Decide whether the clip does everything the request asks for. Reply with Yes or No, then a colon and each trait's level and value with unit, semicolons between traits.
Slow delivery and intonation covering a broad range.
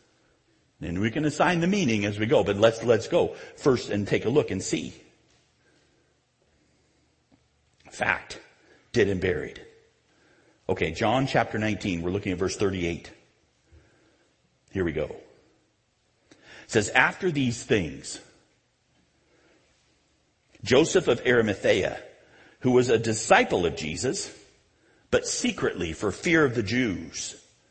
Yes: slow, 125 wpm; wide, 8.8 semitones